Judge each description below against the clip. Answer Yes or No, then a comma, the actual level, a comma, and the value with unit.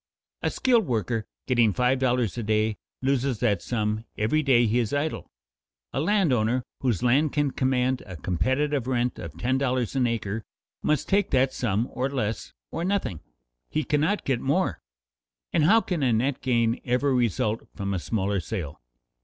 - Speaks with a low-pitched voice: Yes, low, 125 Hz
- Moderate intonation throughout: Yes, average, 3.9 semitones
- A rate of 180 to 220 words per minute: No, average, 165 wpm